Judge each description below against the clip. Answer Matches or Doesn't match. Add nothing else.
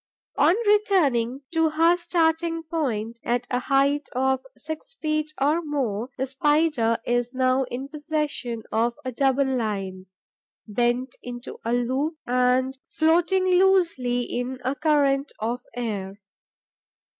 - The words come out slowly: Matches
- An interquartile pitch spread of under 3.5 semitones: Doesn't match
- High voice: Matches